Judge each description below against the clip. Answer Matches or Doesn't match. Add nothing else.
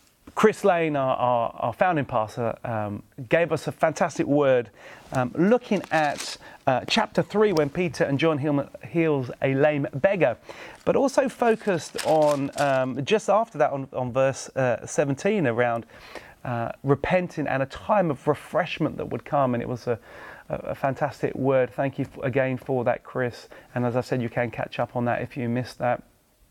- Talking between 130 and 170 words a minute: Doesn't match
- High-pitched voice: Doesn't match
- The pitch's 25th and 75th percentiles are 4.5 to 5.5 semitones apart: Matches